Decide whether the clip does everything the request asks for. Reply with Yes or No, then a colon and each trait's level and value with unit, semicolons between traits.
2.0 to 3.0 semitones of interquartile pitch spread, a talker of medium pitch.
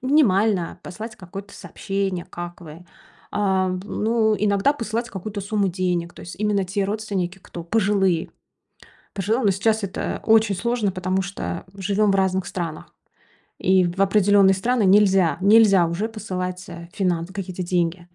No: narrow, 2.5 semitones; high, 195 Hz